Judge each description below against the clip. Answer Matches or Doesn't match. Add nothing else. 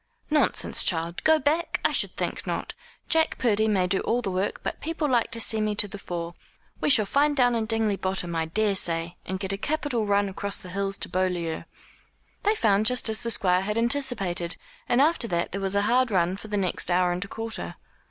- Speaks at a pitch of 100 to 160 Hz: Doesn't match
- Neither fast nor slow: Doesn't match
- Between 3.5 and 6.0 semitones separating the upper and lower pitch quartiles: Matches